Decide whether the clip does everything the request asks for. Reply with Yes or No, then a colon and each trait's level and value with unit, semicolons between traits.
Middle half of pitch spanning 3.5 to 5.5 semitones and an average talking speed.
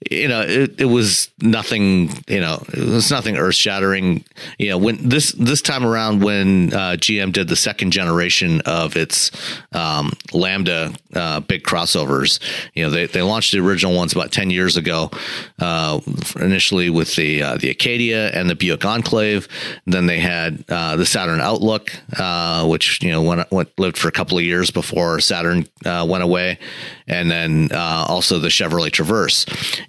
Yes: average, 3.9 semitones; average, 185 wpm